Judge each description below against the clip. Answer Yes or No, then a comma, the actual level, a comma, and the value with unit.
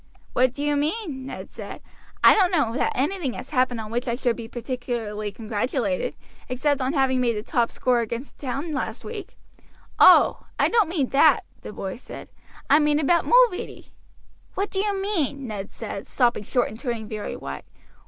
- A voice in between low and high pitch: No, very high, 260 Hz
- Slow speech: No, average, 185 wpm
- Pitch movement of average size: Yes, average, 4.4 semitones